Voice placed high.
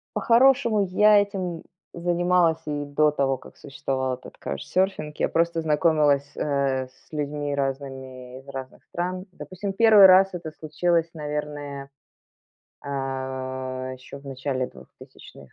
No: medium, 145 Hz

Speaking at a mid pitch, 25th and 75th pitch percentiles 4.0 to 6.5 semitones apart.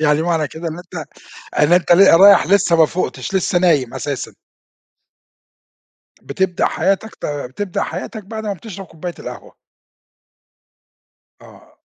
No: medium, 175 Hz; average, 3.5 semitones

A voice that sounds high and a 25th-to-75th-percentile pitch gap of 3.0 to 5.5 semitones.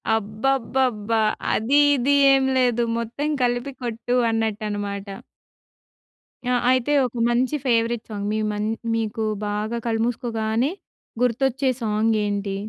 No: high, 230 Hz; narrow, 2.5 semitones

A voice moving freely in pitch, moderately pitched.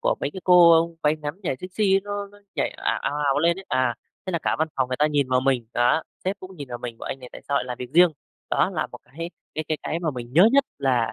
Yes: wide, 5.7 semitones; medium, 150 Hz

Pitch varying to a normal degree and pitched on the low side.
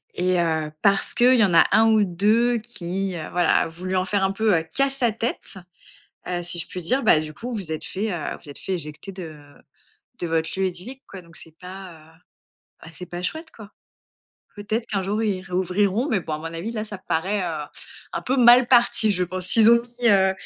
No: average, 4.2 semitones; high, 190 Hz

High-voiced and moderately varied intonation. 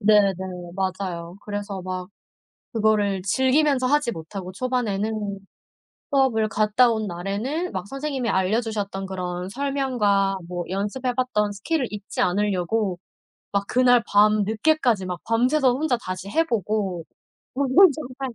Yes: high, 210 Hz; average, 4.6 semitones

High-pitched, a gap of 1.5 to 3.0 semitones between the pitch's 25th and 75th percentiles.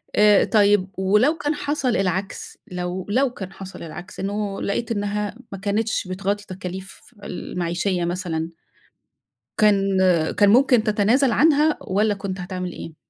Yes: high, 200 Hz; narrow, 2.5 semitones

